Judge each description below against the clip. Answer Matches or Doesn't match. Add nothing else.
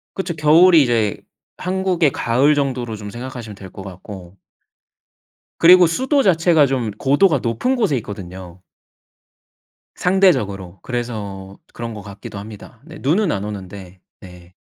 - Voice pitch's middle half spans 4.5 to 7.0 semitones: Doesn't match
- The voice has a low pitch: Matches